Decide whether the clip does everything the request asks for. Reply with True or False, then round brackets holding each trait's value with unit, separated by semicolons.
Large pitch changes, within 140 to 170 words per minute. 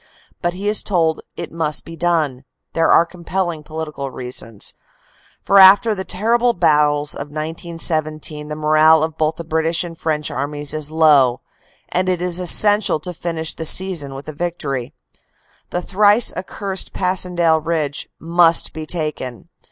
False (2.8 semitones; 160 wpm)